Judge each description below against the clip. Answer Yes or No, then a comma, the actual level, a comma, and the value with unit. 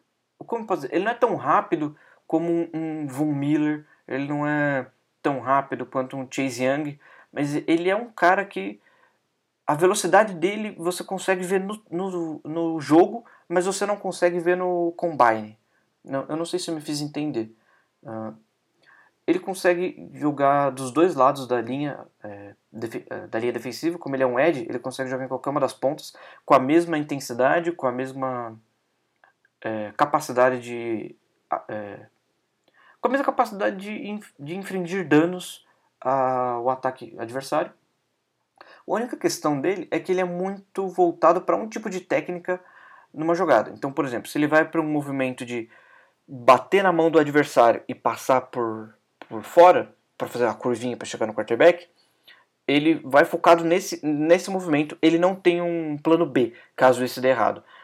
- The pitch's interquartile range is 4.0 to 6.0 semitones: Yes, average, 5.3 semitones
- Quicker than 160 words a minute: Yes, average, 170 wpm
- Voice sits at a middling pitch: Yes, medium, 150 Hz